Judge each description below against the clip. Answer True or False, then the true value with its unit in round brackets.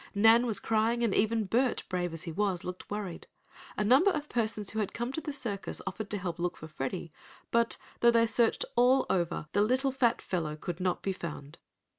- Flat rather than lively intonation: False (4.7 semitones)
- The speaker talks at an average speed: False (210 wpm)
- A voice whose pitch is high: True (210 Hz)